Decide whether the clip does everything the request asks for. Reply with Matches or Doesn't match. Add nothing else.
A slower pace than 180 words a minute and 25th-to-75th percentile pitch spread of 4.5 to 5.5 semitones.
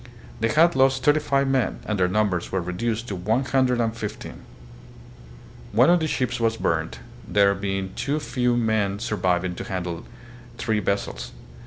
Matches